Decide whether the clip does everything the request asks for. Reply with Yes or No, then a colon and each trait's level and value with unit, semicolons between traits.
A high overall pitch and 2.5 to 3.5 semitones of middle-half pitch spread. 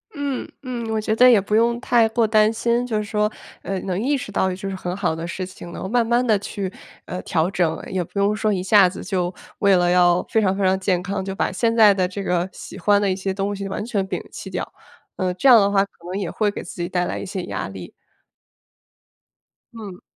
Yes: high, 200 Hz; average, 3.0 semitones